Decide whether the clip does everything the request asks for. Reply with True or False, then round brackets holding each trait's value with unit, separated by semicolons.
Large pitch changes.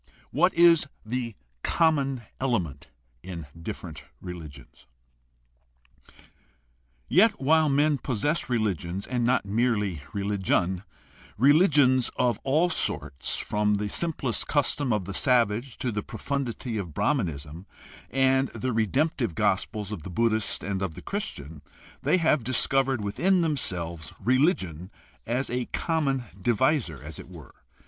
True (6.6 semitones)